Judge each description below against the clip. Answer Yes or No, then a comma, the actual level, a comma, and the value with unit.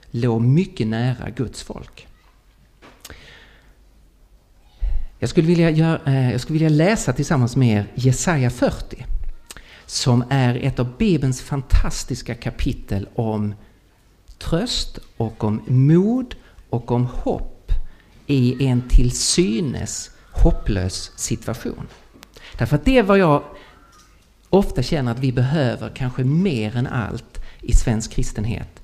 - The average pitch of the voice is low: Yes, low, 125 Hz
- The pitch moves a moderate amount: Yes, average, 4.3 semitones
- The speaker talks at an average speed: No, slow, 110 wpm